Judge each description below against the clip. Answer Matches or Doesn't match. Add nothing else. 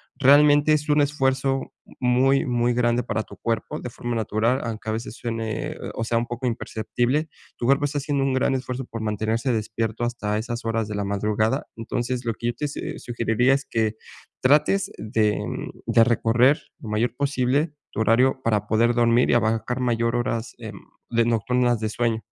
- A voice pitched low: Matches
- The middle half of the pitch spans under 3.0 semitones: Matches